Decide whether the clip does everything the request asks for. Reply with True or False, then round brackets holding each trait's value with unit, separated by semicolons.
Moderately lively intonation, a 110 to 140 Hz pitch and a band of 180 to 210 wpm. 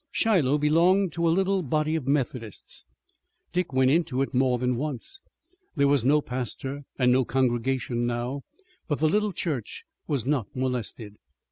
False (3.9 semitones; 135 Hz; 155 wpm)